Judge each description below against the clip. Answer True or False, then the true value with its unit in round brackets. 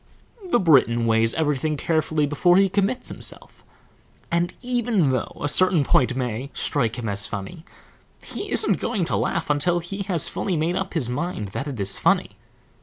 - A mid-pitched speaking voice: True (150 Hz)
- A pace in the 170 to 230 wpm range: True (175 wpm)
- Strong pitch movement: True (6.3 semitones)